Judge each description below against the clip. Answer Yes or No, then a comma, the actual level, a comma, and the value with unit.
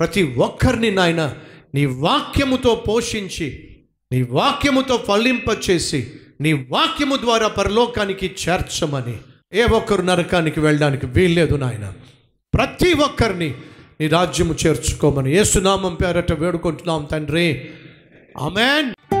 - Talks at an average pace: Yes, average, 95 wpm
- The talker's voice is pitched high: No, medium, 175 Hz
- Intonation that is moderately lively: No, wide, 5.8 semitones